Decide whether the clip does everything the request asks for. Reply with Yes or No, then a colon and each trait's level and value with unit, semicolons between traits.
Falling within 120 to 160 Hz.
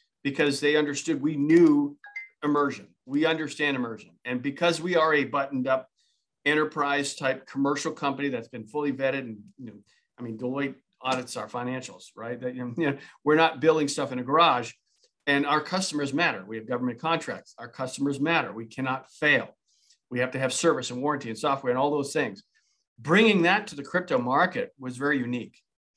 Yes: medium, 140 Hz